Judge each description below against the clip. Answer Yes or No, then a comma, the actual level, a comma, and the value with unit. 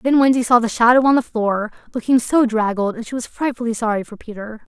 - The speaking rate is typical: No, fast, 225 wpm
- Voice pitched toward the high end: Yes, high, 235 Hz